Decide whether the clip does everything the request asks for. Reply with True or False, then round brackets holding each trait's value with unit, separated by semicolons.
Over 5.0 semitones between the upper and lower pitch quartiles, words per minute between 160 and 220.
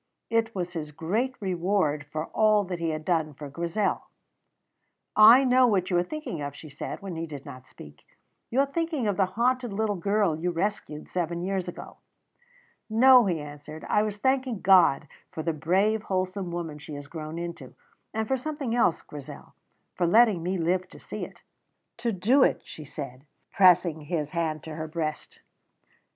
True (5.4 semitones; 180 wpm)